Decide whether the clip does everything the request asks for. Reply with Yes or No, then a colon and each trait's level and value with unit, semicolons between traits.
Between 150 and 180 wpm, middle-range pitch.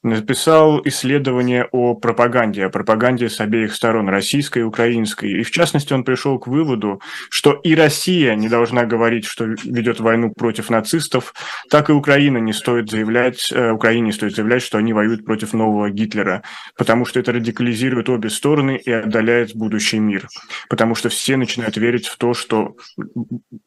No: fast, 160 wpm; low, 120 Hz